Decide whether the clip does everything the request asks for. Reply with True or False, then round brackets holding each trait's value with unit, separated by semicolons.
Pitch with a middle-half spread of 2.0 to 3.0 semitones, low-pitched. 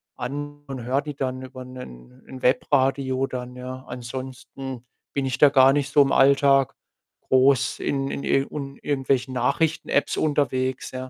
False (1.4 semitones; 130 Hz)